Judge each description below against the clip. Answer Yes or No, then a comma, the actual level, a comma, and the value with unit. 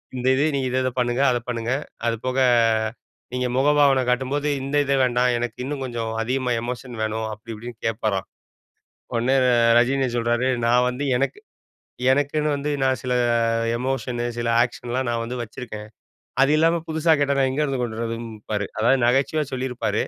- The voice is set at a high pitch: No, low, 125 Hz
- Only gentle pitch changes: Yes, narrow, 2.3 semitones